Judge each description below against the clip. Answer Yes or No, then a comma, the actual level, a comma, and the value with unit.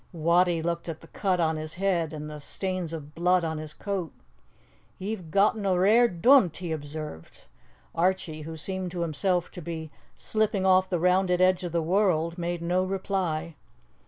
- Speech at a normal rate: Yes, average, 175 wpm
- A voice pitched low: No, medium, 175 Hz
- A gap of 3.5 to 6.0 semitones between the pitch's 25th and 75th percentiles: No, average, 2.7 semitones